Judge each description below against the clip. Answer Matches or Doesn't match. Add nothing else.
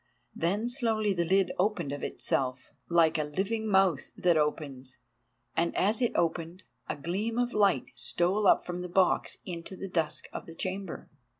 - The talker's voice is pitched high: Doesn't match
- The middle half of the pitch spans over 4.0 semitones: Doesn't match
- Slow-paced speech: Doesn't match